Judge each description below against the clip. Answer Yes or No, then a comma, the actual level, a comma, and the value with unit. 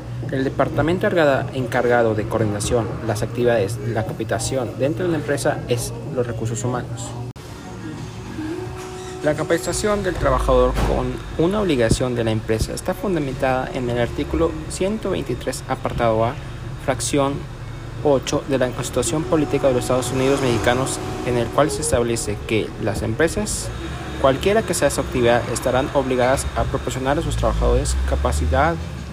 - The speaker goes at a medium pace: Yes, average, 140 wpm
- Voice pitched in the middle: No, low, 125 Hz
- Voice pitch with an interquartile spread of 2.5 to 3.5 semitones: Yes, average, 3.2 semitones